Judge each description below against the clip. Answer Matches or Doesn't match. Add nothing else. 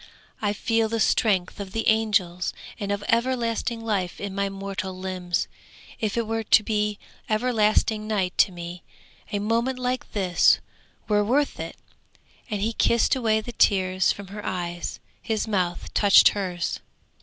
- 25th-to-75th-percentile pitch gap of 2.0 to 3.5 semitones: Matches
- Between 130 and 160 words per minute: Matches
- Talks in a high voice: Matches